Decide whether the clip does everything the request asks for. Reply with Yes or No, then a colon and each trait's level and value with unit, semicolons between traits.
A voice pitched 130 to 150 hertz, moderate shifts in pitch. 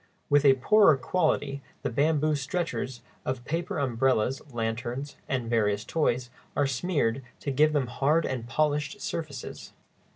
Yes: medium, 140 Hz; average, 3.8 semitones